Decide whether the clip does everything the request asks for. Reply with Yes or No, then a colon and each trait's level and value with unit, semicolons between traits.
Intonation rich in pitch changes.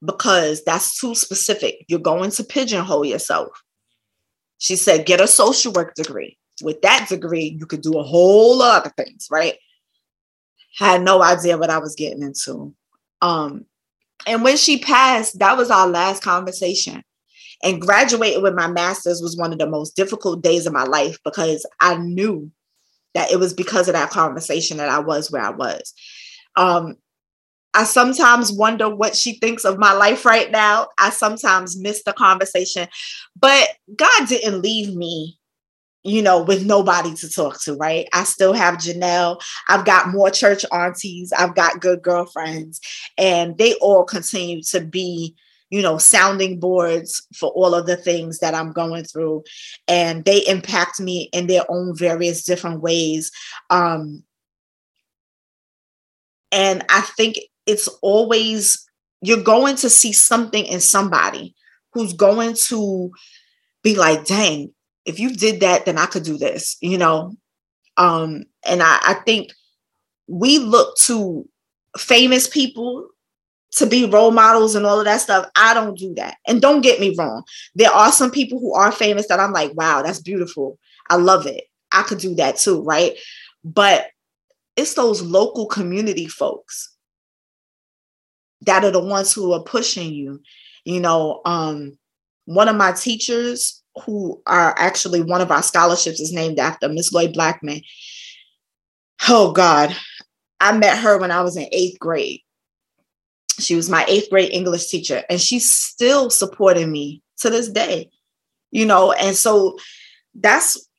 No: average, 4.4 semitones